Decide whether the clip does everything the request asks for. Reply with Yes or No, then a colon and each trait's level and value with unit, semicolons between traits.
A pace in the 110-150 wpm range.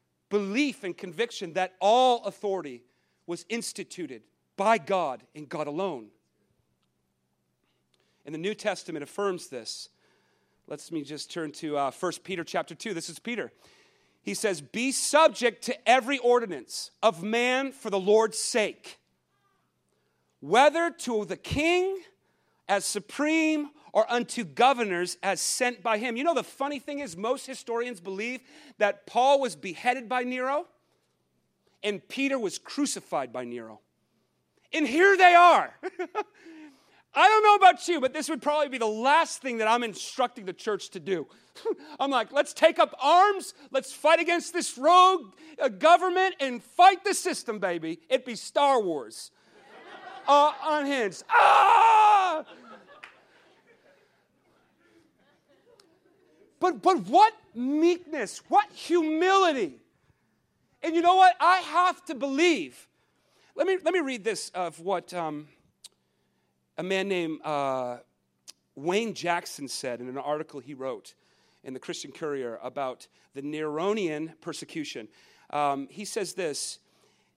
Yes: slow, 135 wpm